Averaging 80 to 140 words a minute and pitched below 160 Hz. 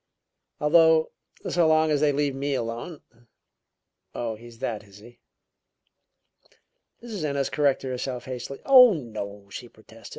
Yes: slow, 135 wpm; low, 135 Hz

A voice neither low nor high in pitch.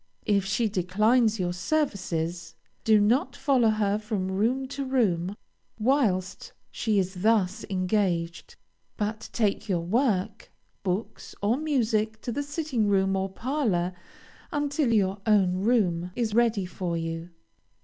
No: high, 210 Hz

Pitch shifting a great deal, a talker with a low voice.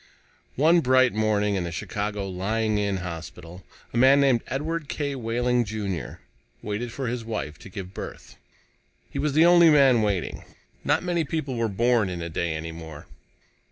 Yes: wide, 6.0 semitones; low, 110 Hz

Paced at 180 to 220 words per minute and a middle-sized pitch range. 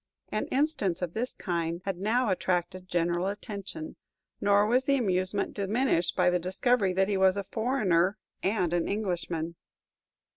No: average, 150 wpm; average, 3.5 semitones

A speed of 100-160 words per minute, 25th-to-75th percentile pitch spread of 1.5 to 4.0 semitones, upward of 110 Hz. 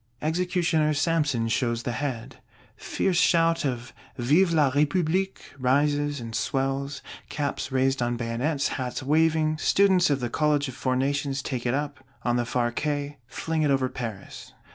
Yes: average, 155 wpm; average, 3.5 semitones; medium, 140 Hz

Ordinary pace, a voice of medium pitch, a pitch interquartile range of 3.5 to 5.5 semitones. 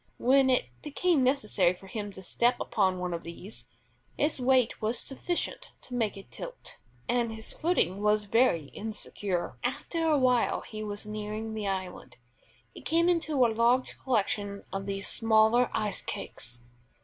No: average, 160 wpm; high, 220 Hz; average, 4.5 semitones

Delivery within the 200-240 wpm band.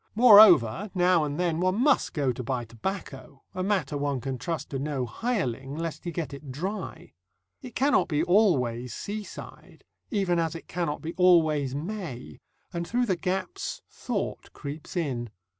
No: average, 160 wpm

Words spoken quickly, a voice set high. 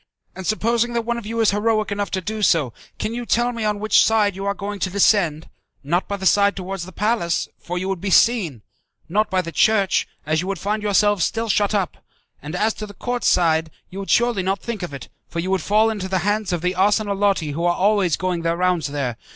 Yes: fast, 240 wpm; high, 195 Hz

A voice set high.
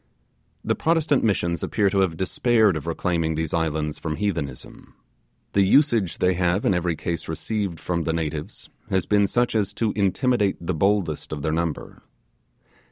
No: very low, 90 Hz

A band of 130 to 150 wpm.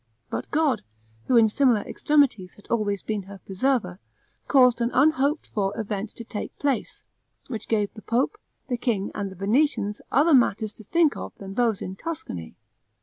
No: average, 170 wpm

